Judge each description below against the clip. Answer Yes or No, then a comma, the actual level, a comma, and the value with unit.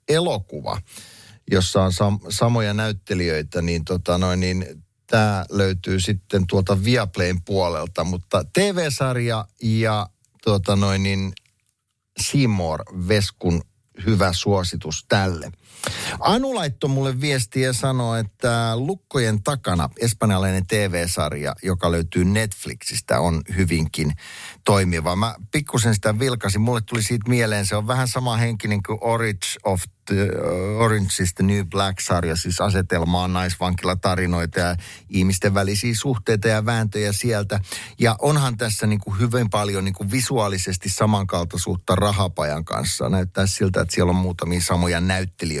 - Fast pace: No, average, 125 wpm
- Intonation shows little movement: No, average, 3.7 semitones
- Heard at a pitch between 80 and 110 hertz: Yes, low, 100 Hz